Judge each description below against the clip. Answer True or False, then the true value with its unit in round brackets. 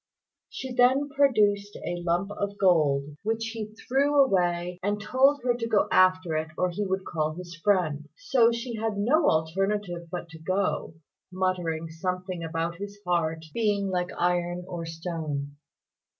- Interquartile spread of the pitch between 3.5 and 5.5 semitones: True (4.0 semitones)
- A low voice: False (185 Hz)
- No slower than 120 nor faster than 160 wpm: True (155 wpm)